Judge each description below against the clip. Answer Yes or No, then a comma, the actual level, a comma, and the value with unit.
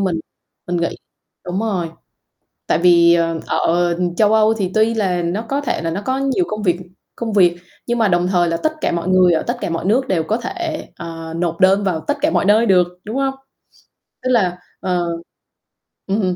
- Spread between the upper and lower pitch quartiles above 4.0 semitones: Yes, average, 4.4 semitones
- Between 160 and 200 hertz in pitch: Yes, high, 190 Hz